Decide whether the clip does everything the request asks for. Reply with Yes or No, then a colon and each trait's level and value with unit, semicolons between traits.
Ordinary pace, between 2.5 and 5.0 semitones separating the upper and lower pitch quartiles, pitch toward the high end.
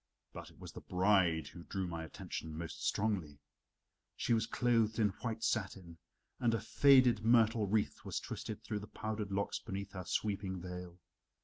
No: average, 170 wpm; average, 3.6 semitones; low, 100 Hz